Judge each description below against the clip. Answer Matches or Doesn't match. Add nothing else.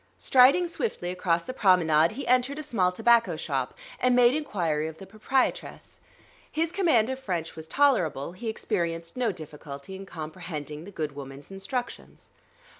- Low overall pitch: Doesn't match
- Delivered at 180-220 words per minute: Doesn't match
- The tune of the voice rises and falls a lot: Matches